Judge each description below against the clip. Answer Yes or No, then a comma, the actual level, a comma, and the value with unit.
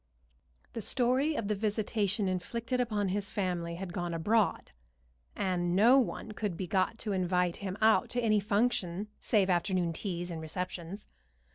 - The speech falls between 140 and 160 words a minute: Yes, average, 155 wpm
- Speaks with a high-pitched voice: Yes, high, 200 Hz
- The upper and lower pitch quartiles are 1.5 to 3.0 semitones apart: No, average, 3.5 semitones